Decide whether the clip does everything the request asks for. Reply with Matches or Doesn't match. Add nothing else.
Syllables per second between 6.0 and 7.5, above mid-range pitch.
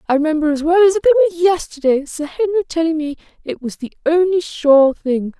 Matches